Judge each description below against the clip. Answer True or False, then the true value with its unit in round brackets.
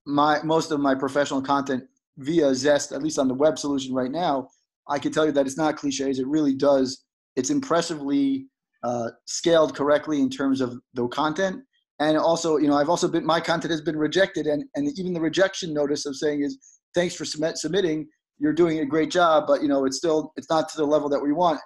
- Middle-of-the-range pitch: True (150 Hz)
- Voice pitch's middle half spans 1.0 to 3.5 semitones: True (2.9 semitones)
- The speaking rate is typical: False (220 wpm)